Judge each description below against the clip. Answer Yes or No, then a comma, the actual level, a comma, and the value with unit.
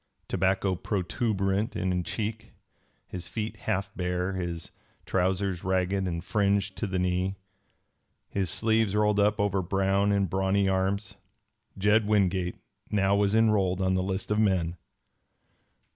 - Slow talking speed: Yes, slow, 130 wpm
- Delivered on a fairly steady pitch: Yes, narrow, 1.7 semitones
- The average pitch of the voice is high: No, very low, 95 Hz